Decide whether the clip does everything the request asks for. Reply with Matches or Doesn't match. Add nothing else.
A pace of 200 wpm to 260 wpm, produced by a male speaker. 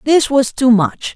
Doesn't match